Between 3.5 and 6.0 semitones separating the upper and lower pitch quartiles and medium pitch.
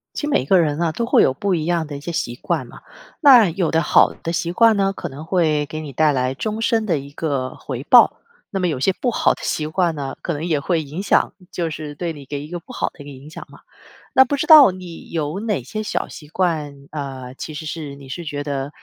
Yes: average, 4.3 semitones; medium, 160 Hz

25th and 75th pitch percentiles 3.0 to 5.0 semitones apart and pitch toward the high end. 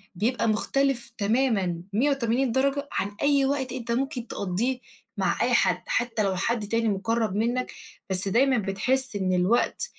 Yes: average, 4.5 semitones; high, 235 Hz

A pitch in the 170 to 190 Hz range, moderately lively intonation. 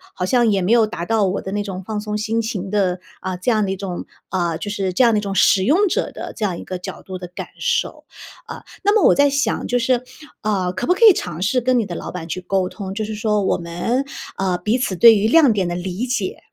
No: high, 205 Hz; average, 4.0 semitones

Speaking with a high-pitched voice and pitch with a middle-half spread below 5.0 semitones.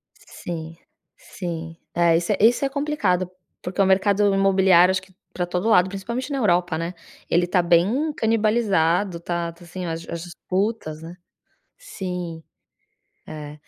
No: medium, 180 Hz; average, 3.2 semitones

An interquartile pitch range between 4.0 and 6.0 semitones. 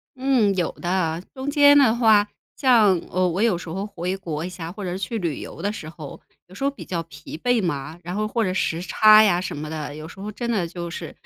Yes: average, 4.5 semitones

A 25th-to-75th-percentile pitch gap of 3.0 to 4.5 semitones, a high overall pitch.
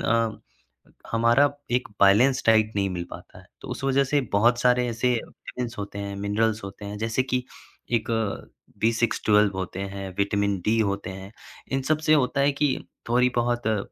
No: average, 3.6 semitones; low, 115 Hz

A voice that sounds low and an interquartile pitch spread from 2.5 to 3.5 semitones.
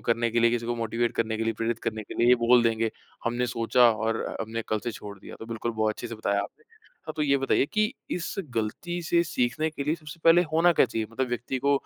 No: low, 120 Hz; average, 3.9 semitones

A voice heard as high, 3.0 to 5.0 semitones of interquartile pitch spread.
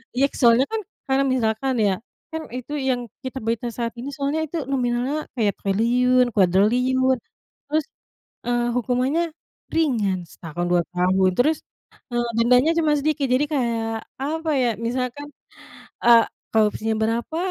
Yes: high, 245 Hz; average, 3.4 semitones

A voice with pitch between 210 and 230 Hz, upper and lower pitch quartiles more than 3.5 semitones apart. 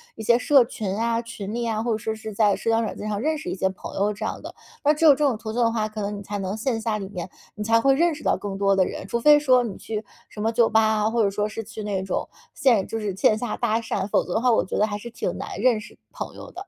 No: high, 220 Hz; narrow, 2.4 semitones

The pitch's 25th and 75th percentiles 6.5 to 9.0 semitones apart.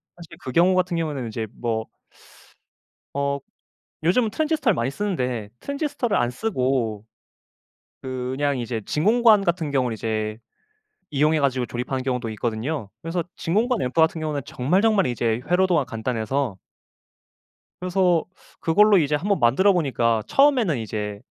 Yes: wide, 7.3 semitones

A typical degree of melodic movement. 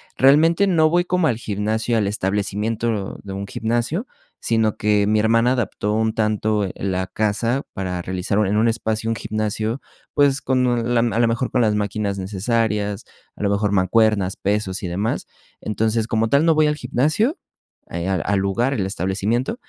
Yes: average, 3.1 semitones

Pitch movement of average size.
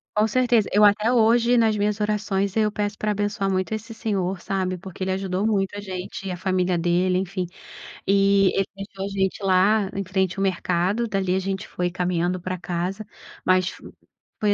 No: narrow, 2.2 semitones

